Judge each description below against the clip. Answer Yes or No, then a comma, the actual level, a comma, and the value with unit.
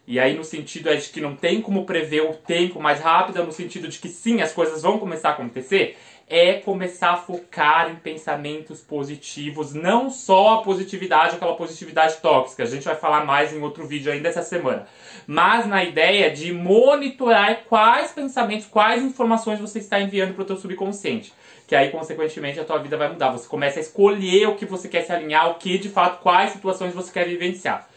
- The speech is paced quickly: Yes, fast, 200 wpm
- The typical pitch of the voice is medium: Yes, medium, 175 Hz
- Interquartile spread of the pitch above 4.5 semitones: No, average, 4.1 semitones